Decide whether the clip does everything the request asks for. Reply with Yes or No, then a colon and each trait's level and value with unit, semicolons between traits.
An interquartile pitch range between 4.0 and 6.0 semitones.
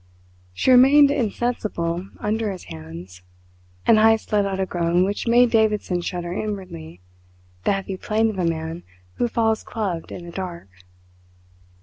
Yes: average, 4.4 semitones